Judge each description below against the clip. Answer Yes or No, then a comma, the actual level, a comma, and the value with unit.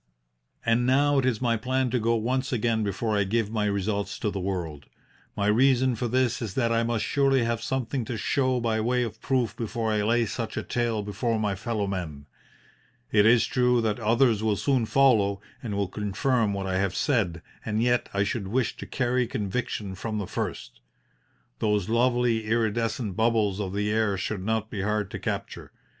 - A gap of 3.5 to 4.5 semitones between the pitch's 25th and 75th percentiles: No, average, 3.1 semitones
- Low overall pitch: Yes, low, 110 Hz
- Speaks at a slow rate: No, average, 195 wpm